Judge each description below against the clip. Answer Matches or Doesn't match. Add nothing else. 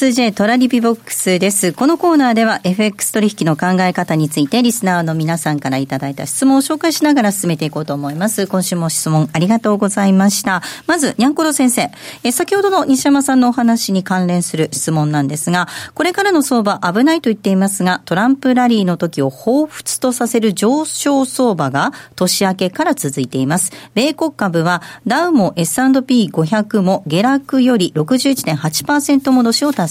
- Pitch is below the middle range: Doesn't match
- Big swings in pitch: Matches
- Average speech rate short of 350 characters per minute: Doesn't match